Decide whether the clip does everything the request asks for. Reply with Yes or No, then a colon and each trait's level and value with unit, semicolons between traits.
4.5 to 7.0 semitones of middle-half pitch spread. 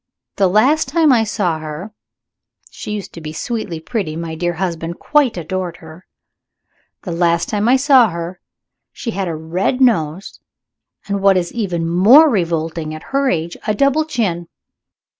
Yes: wide, 5.6 semitones